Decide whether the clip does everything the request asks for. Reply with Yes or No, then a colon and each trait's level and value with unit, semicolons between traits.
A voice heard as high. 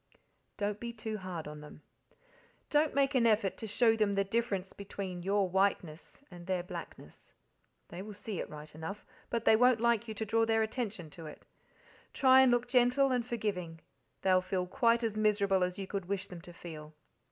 Yes: high, 205 Hz